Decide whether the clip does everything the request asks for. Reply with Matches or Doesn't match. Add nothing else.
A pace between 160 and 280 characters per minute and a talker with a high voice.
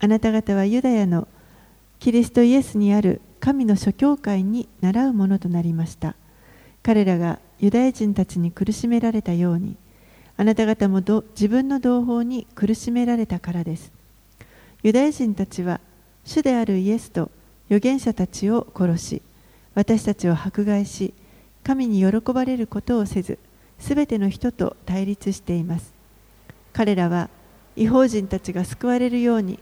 Doesn't match